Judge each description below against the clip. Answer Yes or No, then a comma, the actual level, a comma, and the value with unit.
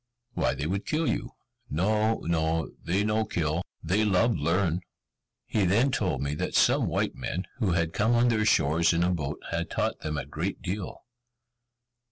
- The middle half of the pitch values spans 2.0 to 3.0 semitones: No, average, 4.7 semitones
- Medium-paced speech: Yes, average, 180 wpm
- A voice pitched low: Yes, very low, 90 Hz